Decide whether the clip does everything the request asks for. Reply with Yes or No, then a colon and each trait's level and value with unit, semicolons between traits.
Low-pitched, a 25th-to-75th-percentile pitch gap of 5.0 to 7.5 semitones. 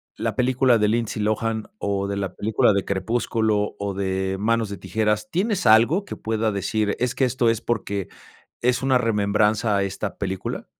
No: low, 110 Hz; average, 2.7 semitones